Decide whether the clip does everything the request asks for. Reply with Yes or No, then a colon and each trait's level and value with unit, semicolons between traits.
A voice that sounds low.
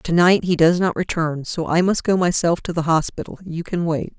No: medium, 170 Hz